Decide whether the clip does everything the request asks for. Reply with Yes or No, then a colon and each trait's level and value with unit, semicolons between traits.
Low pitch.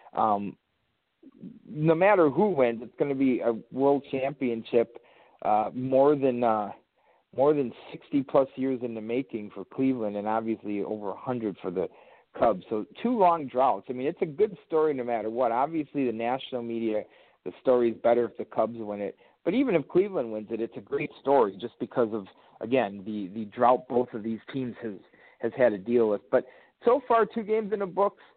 Yes: low, 125 Hz